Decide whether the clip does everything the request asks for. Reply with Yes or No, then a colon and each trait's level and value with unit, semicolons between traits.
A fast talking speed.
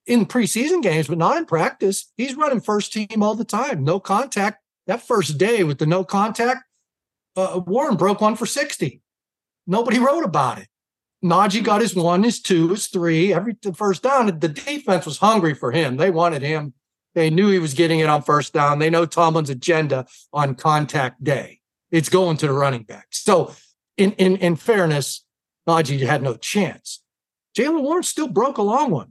No: average, 190 wpm